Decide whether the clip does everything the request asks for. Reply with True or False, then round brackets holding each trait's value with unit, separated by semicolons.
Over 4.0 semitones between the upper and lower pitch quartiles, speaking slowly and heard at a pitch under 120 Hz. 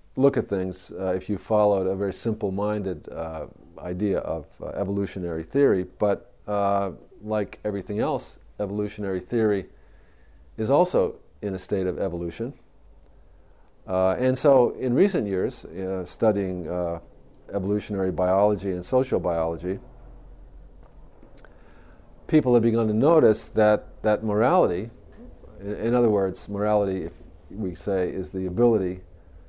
False (2.7 semitones; 130 wpm; 100 Hz)